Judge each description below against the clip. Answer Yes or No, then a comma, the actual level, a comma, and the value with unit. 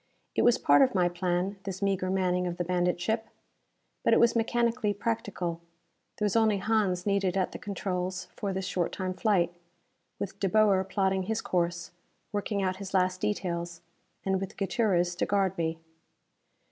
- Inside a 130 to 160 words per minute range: No, average, 170 wpm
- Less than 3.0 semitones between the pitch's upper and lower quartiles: Yes, narrow, 2.4 semitones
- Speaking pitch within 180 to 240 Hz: Yes, high, 190 Hz